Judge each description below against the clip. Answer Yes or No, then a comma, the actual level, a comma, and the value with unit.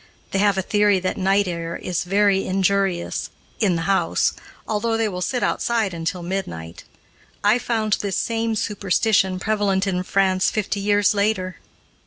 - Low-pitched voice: No, high, 195 Hz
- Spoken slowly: No, average, 155 wpm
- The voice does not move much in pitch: Yes, narrow, 2.1 semitones